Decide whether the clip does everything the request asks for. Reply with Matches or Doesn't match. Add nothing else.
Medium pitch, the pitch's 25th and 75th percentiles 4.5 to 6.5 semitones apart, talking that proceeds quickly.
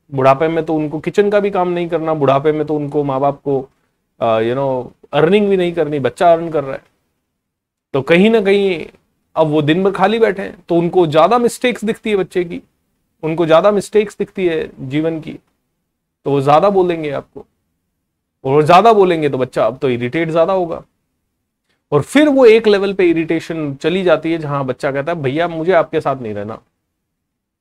Matches